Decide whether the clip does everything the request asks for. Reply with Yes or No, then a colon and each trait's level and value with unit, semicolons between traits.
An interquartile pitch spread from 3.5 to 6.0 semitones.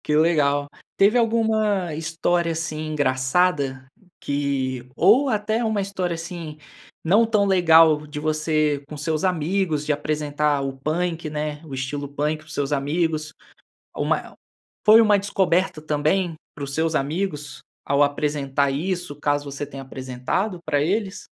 Yes: average, 3.8 semitones